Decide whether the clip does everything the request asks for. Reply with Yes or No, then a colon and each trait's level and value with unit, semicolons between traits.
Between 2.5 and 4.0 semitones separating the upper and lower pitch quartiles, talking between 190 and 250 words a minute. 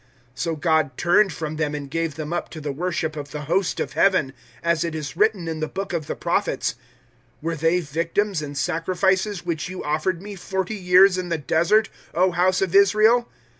Yes: average, 3.3 semitones; fast, 205 wpm